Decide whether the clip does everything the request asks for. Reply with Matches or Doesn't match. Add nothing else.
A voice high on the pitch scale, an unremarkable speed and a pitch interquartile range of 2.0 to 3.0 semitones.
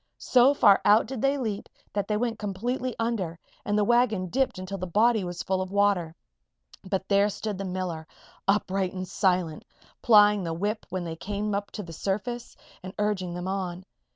Matches